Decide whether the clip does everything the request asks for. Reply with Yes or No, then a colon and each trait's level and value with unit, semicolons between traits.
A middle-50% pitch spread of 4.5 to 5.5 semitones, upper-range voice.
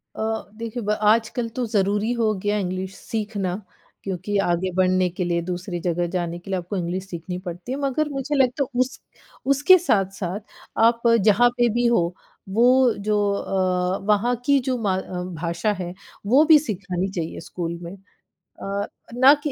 Yes: average, 4.9 semitones; high, 195 Hz